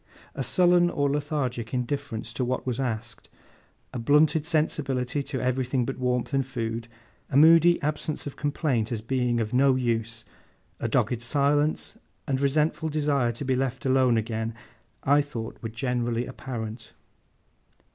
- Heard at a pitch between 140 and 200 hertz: No, low, 130 Hz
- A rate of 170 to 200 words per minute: No, average, 145 wpm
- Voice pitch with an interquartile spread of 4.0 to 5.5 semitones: No, average, 3.6 semitones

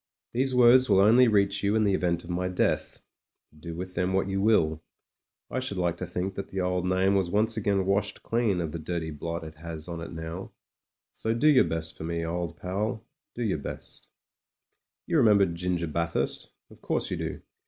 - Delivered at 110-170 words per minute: No, fast, 205 wpm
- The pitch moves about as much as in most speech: Yes, average, 3.6 semitones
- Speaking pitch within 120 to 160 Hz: No, very low, 90 Hz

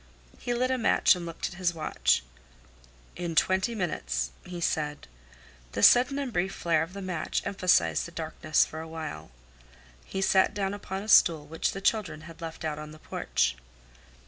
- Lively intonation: No, average, 3.7 semitones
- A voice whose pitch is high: No, medium, 170 Hz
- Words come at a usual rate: Yes, average, 180 wpm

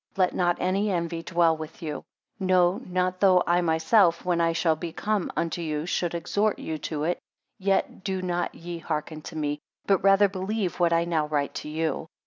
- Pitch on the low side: No, medium, 175 Hz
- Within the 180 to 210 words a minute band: Yes, average, 195 wpm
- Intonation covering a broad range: No, narrow, 2.5 semitones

